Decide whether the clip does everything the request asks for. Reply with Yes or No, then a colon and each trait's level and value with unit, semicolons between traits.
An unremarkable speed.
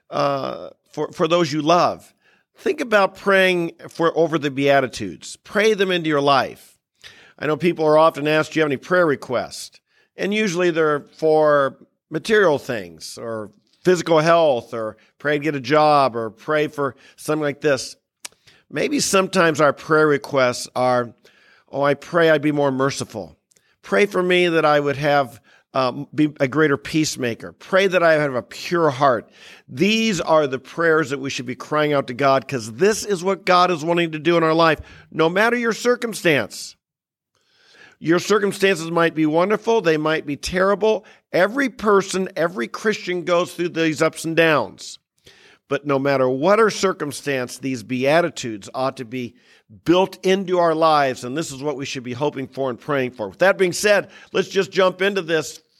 Yes: average, 180 wpm